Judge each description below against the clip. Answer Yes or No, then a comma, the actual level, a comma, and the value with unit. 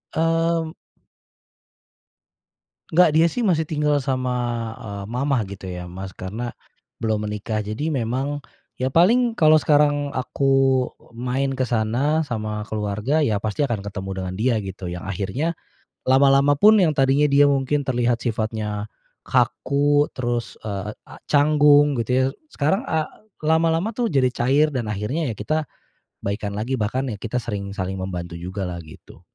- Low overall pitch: Yes, low, 130 Hz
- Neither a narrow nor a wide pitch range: No, wide, 5.7 semitones